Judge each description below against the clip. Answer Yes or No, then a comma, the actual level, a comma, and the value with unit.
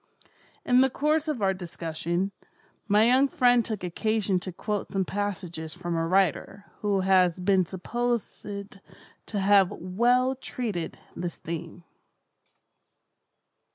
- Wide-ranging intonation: No, average, 4.7 semitones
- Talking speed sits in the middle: No, slow, 120 wpm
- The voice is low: No, high, 195 Hz